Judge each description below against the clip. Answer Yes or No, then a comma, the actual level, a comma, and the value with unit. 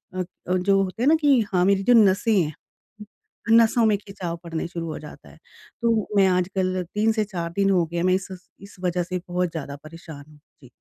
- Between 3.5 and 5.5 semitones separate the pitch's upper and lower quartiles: No, average, 2.9 semitones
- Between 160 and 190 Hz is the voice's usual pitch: Yes, medium, 185 Hz